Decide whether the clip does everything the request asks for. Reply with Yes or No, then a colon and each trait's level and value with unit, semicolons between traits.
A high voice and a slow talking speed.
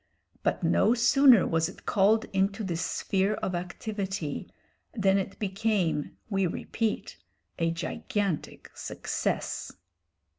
Yes: high, 195 Hz; slow, 110 wpm